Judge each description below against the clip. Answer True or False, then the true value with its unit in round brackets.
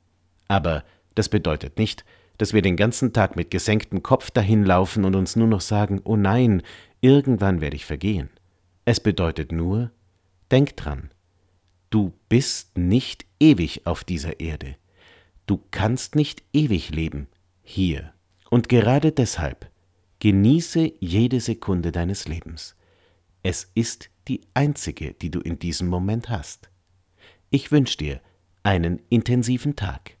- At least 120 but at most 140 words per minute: True (130 wpm)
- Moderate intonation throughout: True (4.5 semitones)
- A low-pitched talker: True (95 Hz)